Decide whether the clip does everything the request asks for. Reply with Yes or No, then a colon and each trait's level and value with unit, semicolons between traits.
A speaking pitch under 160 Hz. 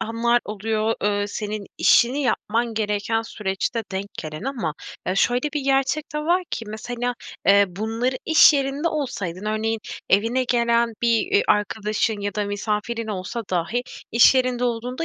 No: high, 225 Hz